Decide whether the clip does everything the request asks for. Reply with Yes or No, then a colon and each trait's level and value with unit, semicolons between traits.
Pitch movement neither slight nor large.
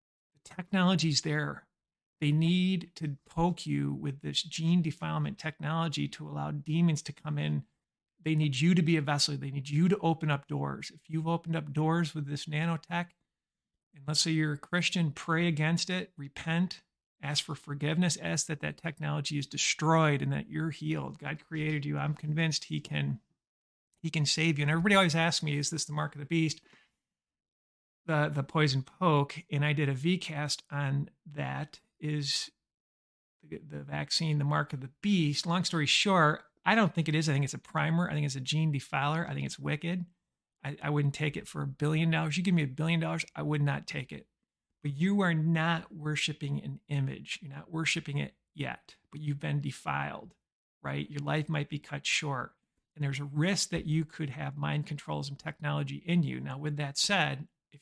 No: narrow, 2.3 semitones